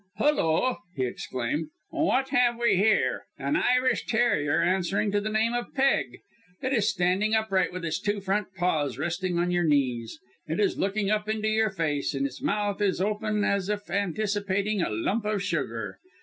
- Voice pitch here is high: Yes, high, 200 Hz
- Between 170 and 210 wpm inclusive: Yes, average, 175 wpm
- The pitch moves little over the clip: No, average, 3.8 semitones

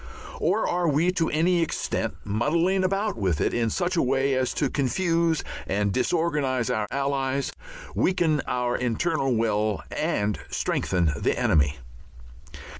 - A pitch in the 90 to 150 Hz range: Yes, medium, 140 Hz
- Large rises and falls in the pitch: Yes, wide, 6.8 semitones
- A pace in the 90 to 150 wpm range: Yes, slow, 135 wpm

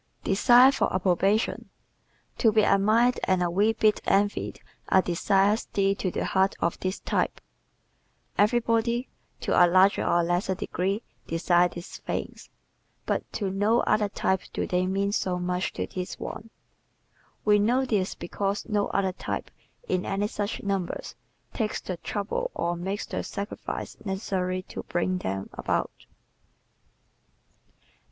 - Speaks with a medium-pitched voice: No, high, 195 Hz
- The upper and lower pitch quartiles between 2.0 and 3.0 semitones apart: Yes, narrow, 2.5 semitones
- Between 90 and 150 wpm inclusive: Yes, average, 145 wpm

